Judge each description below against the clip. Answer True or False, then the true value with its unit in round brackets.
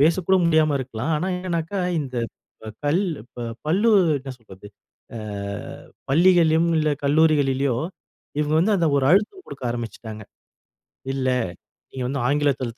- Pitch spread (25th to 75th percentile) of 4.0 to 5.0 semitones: True (4.3 semitones)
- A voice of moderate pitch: True (150 Hz)